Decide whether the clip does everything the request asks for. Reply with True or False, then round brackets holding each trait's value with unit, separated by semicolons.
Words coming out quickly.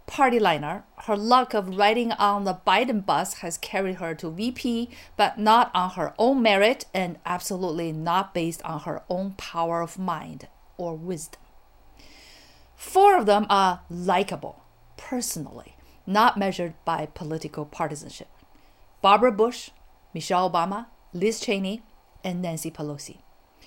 False (135 wpm)